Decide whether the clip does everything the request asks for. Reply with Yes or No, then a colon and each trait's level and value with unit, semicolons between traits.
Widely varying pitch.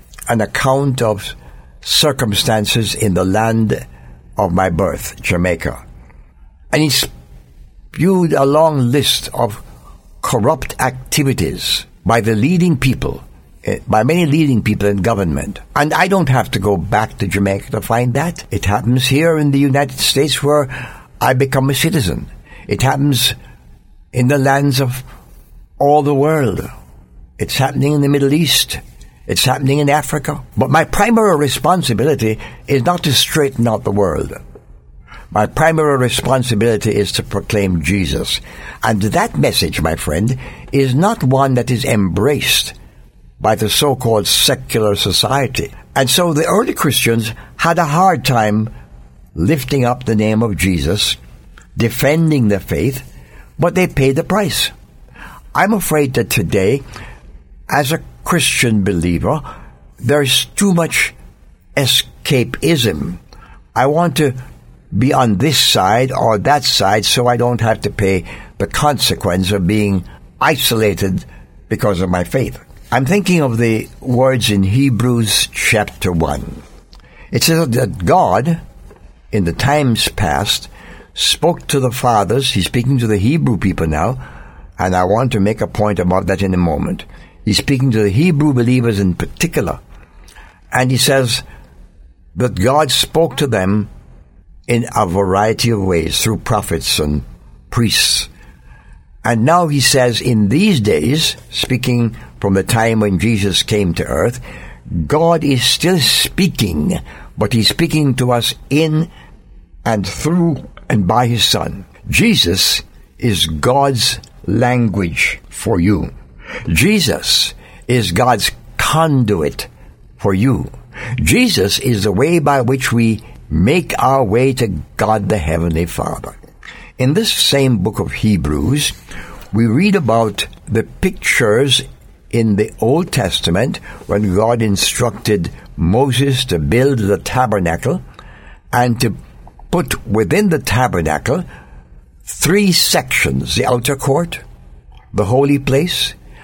Yes: wide, 6.9 semitones